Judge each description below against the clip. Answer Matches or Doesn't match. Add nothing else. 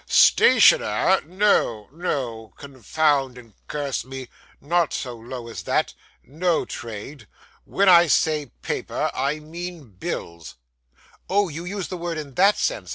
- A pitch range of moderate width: Doesn't match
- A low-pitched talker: Doesn't match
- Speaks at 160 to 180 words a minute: Doesn't match